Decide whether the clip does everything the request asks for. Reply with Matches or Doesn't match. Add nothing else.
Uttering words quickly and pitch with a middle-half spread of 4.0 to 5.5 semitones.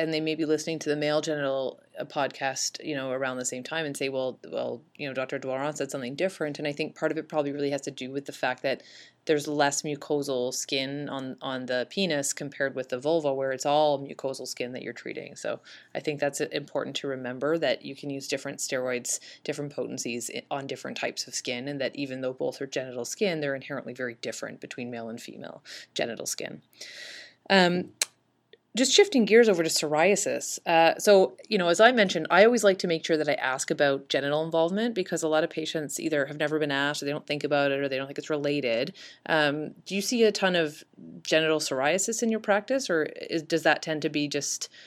Doesn't match